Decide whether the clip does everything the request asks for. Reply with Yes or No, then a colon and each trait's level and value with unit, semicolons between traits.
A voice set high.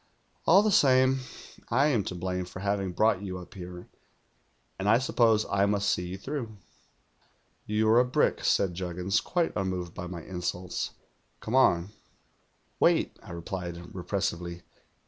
No: very low, 95 Hz